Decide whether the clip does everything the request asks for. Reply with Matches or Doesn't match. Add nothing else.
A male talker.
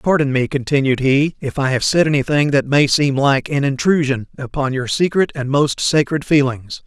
Matches